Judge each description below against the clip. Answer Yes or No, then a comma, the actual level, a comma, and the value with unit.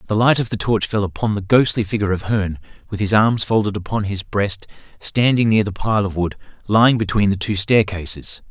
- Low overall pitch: Yes, low, 105 Hz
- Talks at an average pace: No, fast, 210 wpm